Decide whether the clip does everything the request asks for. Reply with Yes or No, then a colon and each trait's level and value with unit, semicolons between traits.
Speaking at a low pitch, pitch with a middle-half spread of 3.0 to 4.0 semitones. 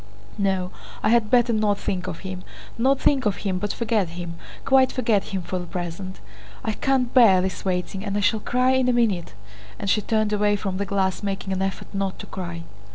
No: high, 200 Hz; average, 3.4 semitones